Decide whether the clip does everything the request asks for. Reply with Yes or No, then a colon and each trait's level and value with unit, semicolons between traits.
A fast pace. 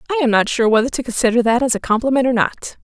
Yes: fast, 275 wpm